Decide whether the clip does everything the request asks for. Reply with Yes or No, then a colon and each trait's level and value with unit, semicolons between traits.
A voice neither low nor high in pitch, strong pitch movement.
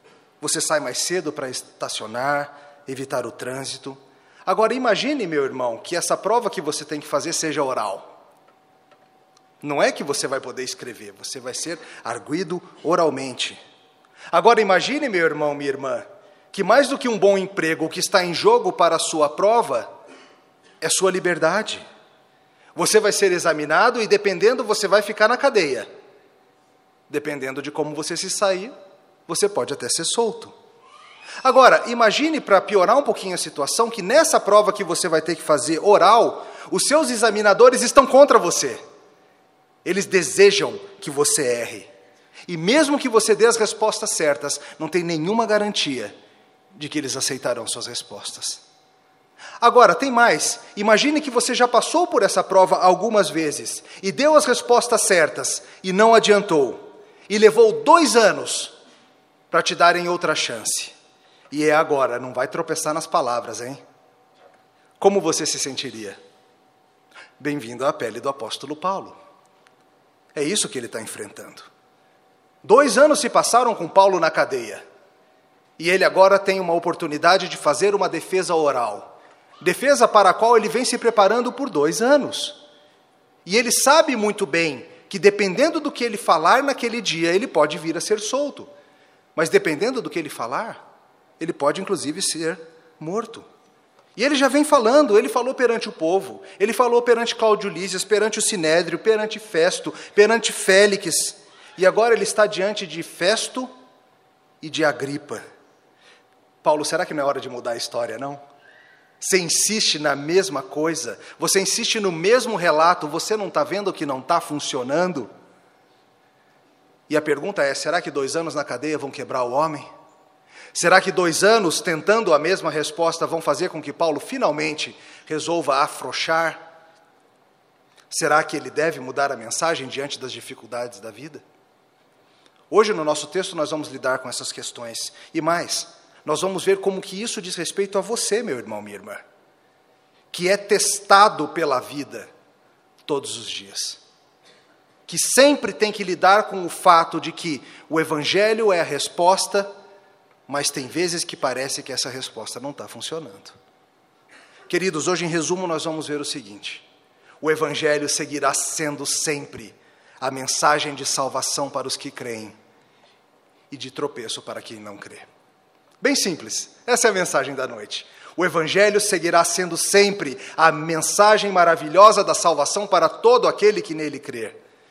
Yes: medium, 180 Hz; wide, 6.1 semitones